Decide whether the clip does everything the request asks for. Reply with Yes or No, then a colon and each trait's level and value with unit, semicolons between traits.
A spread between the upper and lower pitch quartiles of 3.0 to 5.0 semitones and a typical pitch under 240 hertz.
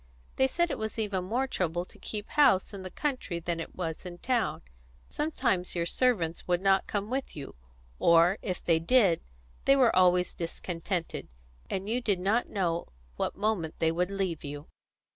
Yes: average, 4.6 semitones; medium, 185 Hz